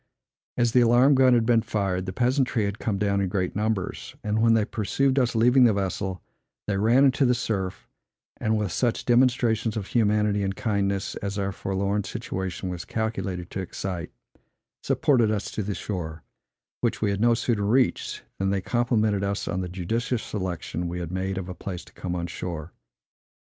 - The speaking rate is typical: Yes, average, 185 wpm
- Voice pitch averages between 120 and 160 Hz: No, low, 105 Hz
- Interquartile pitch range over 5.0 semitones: No, average, 3.5 semitones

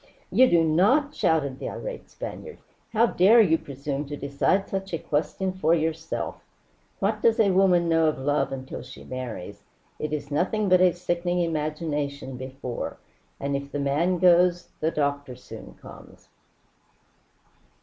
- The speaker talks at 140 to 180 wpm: Yes, average, 150 wpm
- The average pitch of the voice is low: No, medium, 160 Hz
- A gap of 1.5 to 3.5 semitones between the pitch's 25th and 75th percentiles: No, average, 4.5 semitones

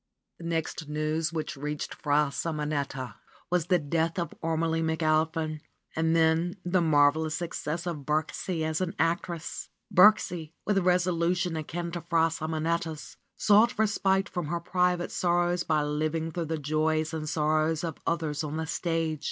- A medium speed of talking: Yes, average, 150 wpm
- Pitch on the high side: No, medium, 160 Hz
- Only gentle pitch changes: Yes, narrow, 1.9 semitones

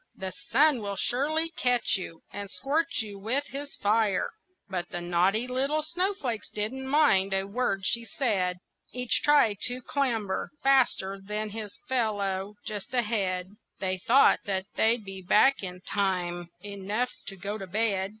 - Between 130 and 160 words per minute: Yes, average, 150 wpm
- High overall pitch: Yes, high, 210 Hz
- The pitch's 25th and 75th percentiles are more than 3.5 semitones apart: Yes, average, 4.8 semitones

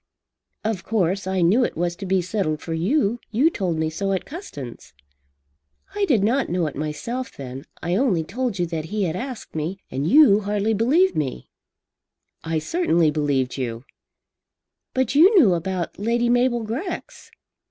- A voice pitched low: No, high, 195 Hz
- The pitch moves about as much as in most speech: No, wide, 6.9 semitones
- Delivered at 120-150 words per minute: No, average, 165 wpm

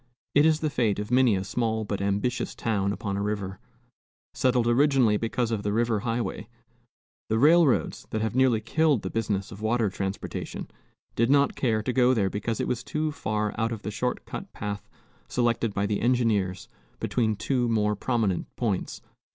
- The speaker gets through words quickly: No, average, 180 wpm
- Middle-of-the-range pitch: No, low, 115 Hz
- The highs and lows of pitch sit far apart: No, average, 3.3 semitones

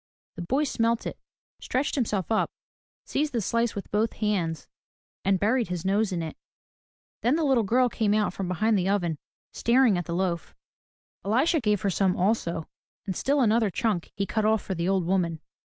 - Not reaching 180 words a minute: No, average, 190 wpm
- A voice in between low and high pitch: No, high, 210 Hz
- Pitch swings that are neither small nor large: Yes, average, 4.2 semitones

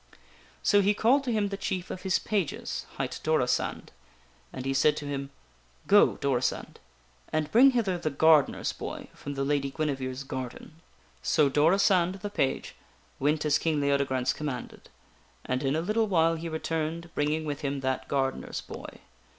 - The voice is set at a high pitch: No, medium, 150 Hz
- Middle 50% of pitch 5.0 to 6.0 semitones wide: No, average, 4.6 semitones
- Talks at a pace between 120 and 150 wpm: No, average, 165 wpm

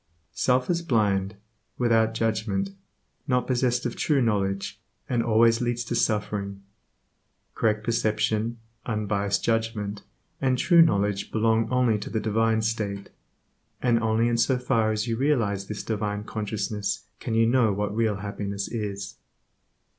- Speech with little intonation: Yes, narrow, 2.3 semitones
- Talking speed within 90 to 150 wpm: Yes, average, 140 wpm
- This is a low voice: Yes, low, 110 Hz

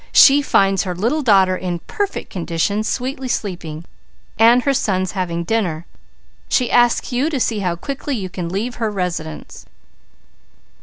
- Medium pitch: No, high, 200 Hz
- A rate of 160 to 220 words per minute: No, average, 150 wpm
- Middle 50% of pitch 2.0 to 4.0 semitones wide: No, wide, 5.5 semitones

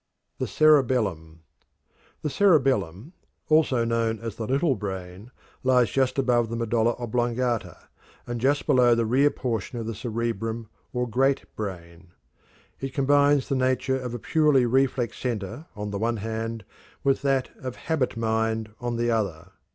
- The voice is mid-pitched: No, low, 120 Hz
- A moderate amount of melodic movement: Yes, average, 3.0 semitones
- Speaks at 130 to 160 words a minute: Yes, average, 150 wpm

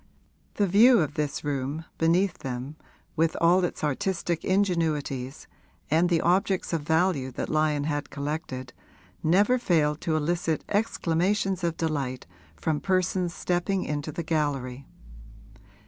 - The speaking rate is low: Yes, slow, 130 wpm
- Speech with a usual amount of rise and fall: Yes, average, 3.6 semitones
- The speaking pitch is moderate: Yes, medium, 160 Hz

